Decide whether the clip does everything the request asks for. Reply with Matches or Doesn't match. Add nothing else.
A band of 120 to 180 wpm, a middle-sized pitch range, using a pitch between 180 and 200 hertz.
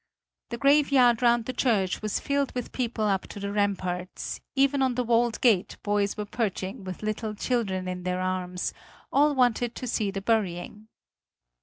Doesn't match